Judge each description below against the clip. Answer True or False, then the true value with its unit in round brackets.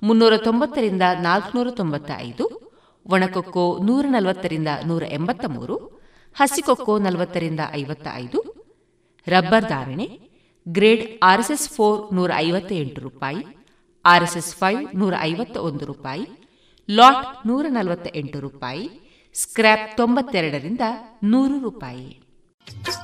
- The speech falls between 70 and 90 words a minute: False (100 wpm)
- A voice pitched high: True (195 Hz)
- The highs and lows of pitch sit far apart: True (6.2 semitones)